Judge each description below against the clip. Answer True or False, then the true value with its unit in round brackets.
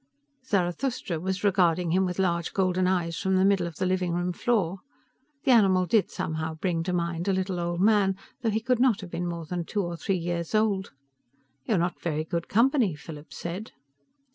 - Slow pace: False (195 wpm)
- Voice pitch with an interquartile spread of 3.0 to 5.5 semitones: False (2.6 semitones)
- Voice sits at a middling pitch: True (180 Hz)